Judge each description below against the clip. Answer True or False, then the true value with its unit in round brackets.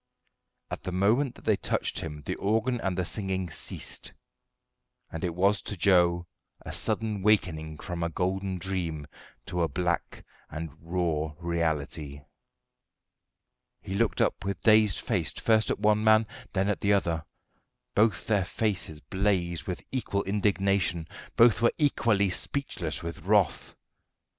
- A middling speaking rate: True (145 wpm)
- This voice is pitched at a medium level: False (95 Hz)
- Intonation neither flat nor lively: True (3.7 semitones)